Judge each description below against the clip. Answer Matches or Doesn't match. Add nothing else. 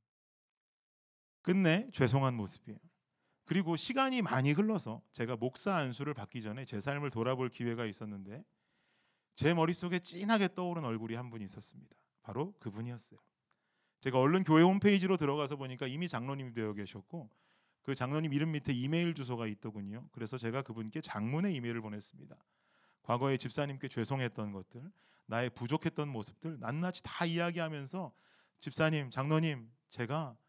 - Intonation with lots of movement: Matches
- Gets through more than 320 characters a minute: Matches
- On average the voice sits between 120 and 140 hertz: Matches